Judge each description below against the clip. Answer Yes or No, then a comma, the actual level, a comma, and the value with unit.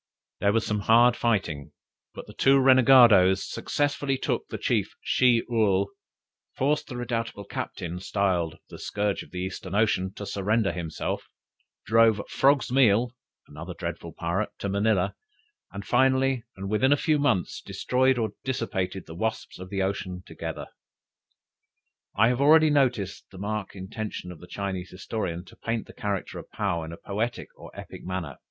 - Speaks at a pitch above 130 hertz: No, low, 105 Hz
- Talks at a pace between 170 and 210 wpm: No, average, 160 wpm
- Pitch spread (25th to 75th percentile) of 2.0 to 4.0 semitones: No, average, 4.6 semitones